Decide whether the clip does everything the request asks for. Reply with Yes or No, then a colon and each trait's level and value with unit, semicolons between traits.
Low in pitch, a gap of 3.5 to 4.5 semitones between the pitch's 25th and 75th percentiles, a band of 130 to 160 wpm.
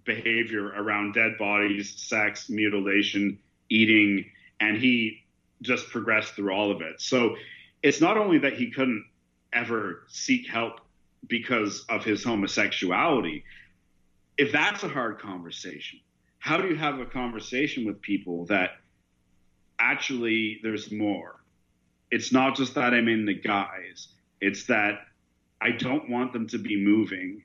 No: low, 105 Hz; average, 2.8 semitones; average, 140 wpm